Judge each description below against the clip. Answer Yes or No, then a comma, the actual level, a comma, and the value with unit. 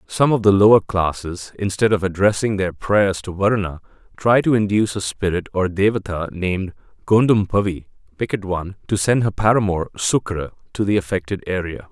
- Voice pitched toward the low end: Yes, low, 100 Hz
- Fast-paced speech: No, average, 160 wpm